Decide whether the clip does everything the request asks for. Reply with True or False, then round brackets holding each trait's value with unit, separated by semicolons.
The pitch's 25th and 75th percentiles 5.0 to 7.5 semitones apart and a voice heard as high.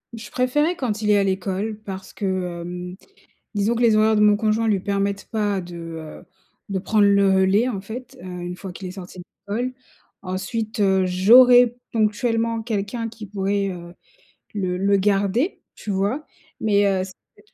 False (2.8 semitones; 200 Hz)